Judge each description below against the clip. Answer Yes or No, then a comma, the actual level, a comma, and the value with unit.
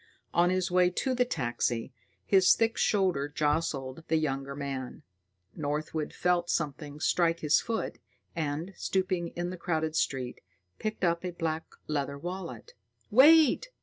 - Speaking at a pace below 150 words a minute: Yes, average, 140 wpm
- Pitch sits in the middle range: Yes, medium, 165 Hz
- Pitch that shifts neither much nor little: Yes, average, 4.1 semitones